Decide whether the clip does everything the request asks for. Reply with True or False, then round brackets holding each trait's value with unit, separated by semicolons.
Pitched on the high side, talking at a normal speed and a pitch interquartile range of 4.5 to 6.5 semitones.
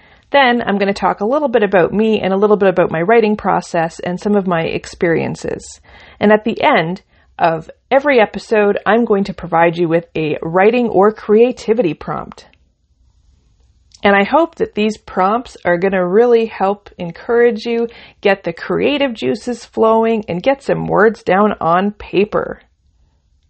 True (200 Hz; 170 wpm; 5.0 semitones)